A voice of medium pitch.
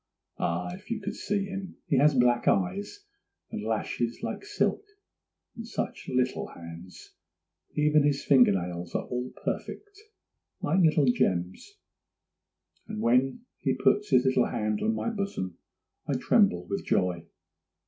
No: low, 130 Hz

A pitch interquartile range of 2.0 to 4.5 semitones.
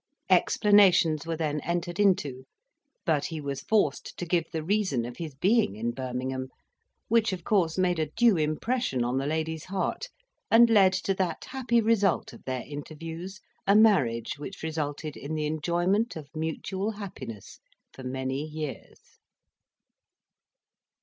No: wide, 5.4 semitones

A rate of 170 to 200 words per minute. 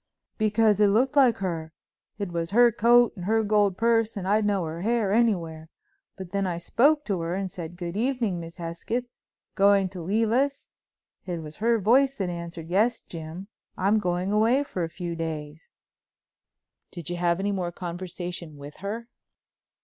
Yes: average, 175 wpm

